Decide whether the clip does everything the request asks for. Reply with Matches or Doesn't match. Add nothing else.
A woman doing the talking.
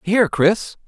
Doesn't match